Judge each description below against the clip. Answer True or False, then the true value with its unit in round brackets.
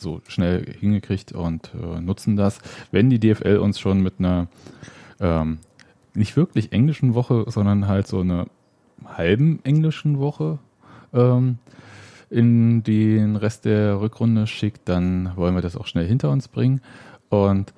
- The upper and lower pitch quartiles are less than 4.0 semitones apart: False (4.5 semitones)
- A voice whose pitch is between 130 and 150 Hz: False (105 Hz)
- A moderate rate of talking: True (140 wpm)